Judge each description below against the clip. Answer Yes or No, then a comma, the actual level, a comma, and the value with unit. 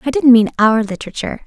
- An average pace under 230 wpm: Yes, fast, 205 wpm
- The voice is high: Yes, high, 235 Hz